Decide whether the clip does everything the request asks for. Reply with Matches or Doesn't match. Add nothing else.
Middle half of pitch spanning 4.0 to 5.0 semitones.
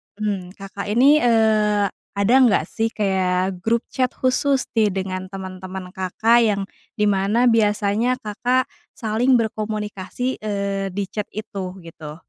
Doesn't match